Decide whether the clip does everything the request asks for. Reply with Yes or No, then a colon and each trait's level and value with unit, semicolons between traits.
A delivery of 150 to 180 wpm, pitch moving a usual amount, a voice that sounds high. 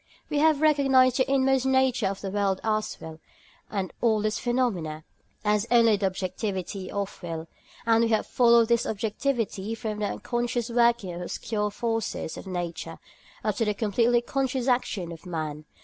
Yes: average, 165 wpm; average, 3.9 semitones; high, 220 Hz